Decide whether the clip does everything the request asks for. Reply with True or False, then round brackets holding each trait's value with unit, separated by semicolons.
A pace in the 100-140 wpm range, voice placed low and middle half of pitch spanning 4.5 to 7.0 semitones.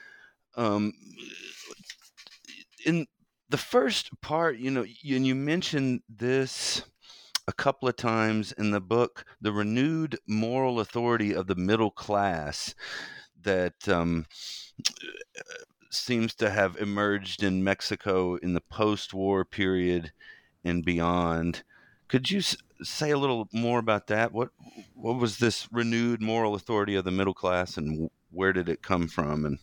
True (135 wpm; 110 Hz; 5.1 semitones)